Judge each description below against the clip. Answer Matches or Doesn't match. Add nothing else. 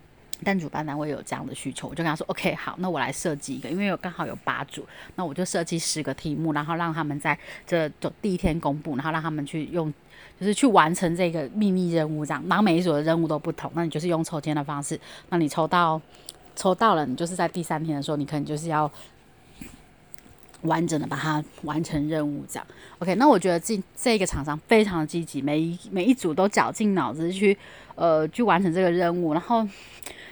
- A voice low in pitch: Doesn't match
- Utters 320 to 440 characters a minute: Matches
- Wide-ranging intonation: Doesn't match